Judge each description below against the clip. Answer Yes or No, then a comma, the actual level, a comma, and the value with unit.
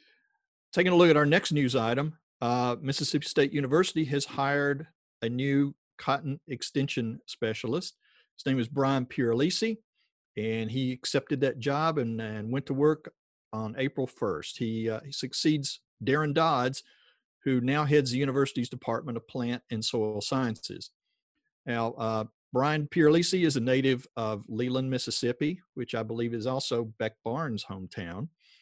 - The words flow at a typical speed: Yes, average, 150 wpm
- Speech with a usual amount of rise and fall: Yes, average, 4.2 semitones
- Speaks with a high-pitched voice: No, low, 130 Hz